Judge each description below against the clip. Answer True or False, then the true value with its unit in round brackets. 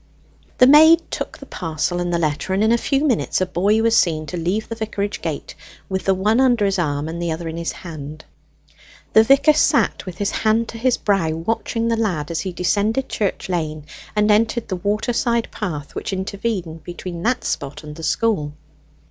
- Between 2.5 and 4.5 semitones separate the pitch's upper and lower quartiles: False (5.2 semitones)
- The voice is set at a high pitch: True (195 Hz)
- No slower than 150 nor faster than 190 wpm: False (200 wpm)